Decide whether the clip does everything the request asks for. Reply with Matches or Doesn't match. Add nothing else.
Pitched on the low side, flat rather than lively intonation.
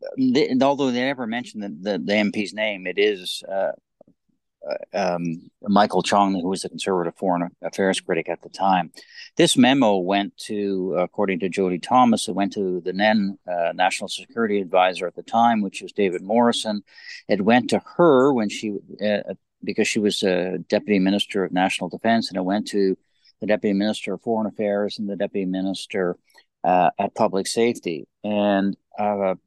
Matches